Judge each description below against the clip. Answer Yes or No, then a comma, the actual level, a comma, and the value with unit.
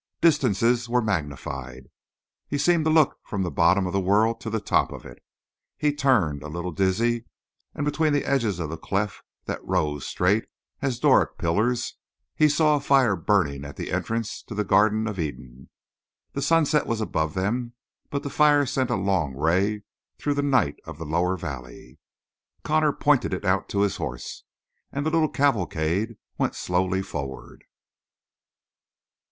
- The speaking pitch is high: No, low, 105 Hz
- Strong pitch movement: Yes, wide, 8.0 semitones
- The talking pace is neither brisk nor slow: Yes, average, 170 wpm